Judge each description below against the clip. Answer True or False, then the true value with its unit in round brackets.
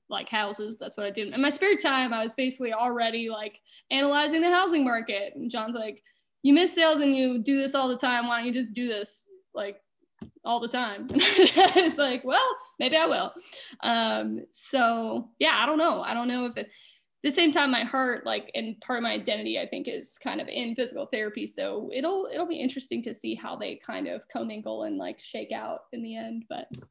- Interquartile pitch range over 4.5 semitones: True (5.4 semitones)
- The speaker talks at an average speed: False (220 wpm)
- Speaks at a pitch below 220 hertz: False (255 Hz)